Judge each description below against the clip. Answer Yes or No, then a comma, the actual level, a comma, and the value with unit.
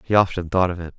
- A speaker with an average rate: No, fast, 305 wpm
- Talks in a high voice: No, very low, 90 Hz